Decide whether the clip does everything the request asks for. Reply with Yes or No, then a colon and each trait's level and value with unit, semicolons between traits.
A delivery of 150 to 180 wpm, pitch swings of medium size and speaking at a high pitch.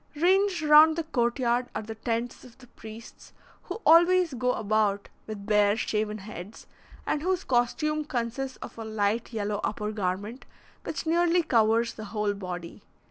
No: average, 160 wpm; wide, 6.1 semitones; high, 230 Hz